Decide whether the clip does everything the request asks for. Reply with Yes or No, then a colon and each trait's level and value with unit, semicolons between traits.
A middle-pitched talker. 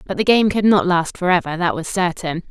Yes: medium, 180 Hz